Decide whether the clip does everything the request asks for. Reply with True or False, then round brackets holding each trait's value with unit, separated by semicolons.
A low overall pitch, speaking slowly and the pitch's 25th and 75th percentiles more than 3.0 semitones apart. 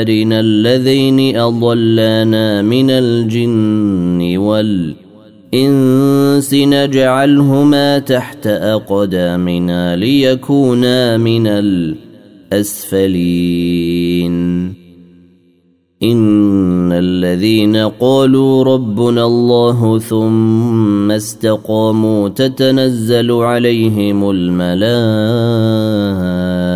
True (110 Hz; 45 wpm; 4.3 semitones)